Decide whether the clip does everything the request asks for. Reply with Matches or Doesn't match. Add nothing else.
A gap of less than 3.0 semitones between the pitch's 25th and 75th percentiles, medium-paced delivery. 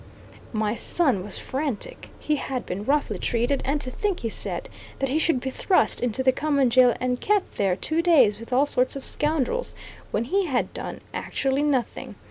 Doesn't match